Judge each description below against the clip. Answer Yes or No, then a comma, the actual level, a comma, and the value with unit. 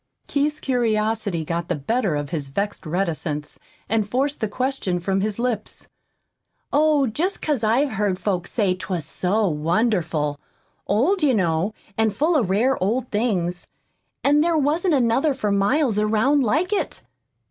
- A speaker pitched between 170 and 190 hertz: No, high, 215 Hz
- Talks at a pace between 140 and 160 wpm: Yes, average, 150 wpm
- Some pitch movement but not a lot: No, wide, 6.6 semitones